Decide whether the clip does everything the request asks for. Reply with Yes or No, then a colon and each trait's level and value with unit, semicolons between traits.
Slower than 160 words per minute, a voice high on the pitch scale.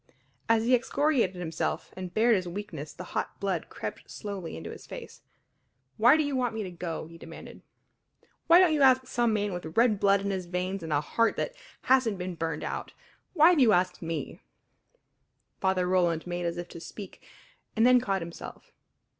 No: average, 190 wpm; high, 195 Hz